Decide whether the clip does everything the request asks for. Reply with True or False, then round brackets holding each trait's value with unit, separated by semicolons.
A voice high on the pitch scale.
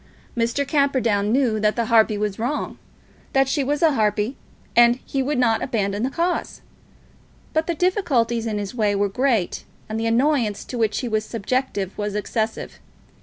True (230 Hz)